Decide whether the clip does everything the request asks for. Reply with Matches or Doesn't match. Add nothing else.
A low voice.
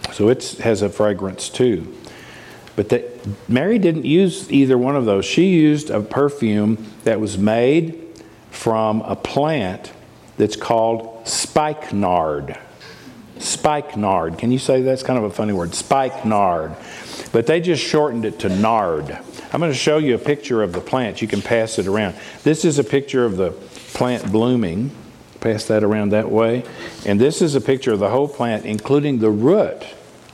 Matches